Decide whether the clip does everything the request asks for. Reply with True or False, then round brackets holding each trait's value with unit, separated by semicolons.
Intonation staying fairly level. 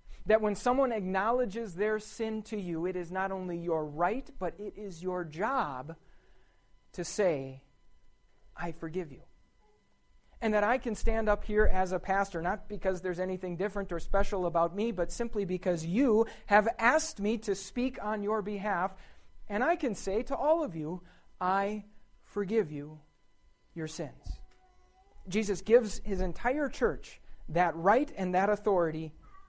False (3.8 semitones)